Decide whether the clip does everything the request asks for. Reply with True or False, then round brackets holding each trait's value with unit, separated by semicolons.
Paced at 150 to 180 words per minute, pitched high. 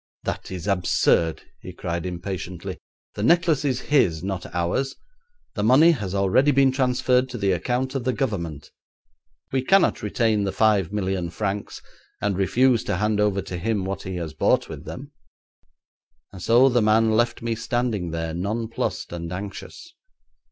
False (160 wpm; 105 Hz)